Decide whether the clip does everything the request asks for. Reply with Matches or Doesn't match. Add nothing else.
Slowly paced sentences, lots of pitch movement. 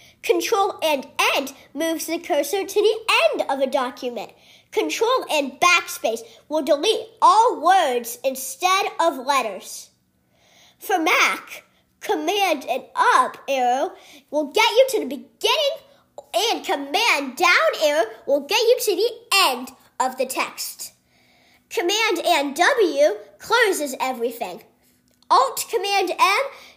Matches